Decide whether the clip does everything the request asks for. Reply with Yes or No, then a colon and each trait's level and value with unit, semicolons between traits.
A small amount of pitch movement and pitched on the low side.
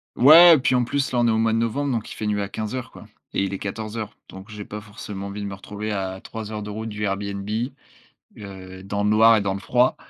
Yes: narrow, 2.2 semitones; low, 105 Hz